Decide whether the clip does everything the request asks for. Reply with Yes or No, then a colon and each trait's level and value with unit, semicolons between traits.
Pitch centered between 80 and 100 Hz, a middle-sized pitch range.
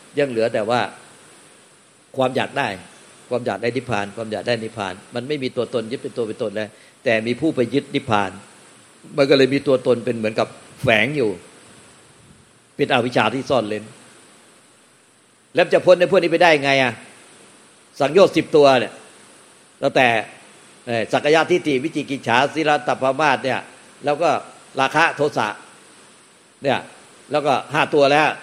No: low, 125 Hz; average, 4.7 semitones